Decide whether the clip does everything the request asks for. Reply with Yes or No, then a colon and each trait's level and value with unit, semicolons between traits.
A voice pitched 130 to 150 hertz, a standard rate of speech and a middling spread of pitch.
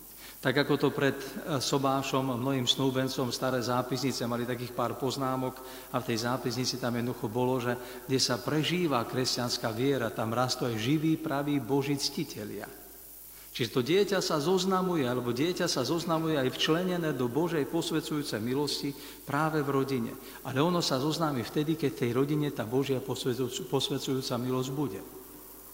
Yes: low, 135 Hz; average, 150 wpm; average, 3.0 semitones